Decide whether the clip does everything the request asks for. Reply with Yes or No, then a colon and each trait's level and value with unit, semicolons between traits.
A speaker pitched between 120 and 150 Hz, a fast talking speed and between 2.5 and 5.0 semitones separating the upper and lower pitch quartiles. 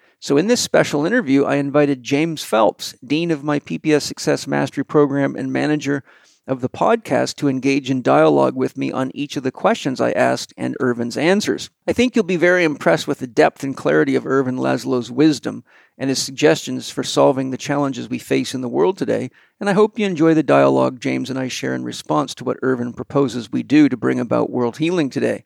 Yes: medium, 140 Hz; fast, 210 wpm; average, 3.6 semitones